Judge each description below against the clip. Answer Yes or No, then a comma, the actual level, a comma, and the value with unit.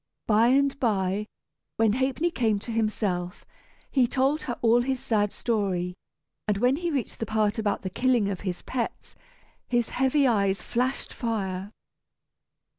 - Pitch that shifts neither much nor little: Yes, average, 4.2 semitones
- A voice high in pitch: Yes, high, 225 Hz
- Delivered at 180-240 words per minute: No, average, 150 wpm